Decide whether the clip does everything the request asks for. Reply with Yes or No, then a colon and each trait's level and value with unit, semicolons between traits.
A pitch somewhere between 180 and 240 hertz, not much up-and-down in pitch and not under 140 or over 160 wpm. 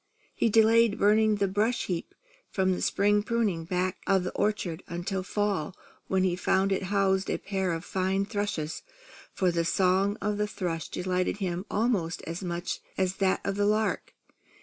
No: high, 190 Hz; narrow, 2.3 semitones; average, 170 wpm